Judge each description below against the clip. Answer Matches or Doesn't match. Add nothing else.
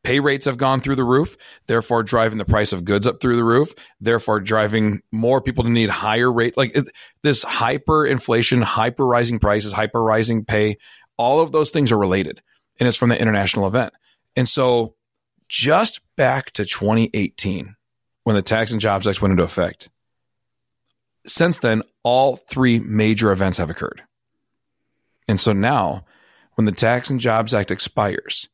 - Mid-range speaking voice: Doesn't match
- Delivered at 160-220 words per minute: Matches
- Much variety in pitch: Doesn't match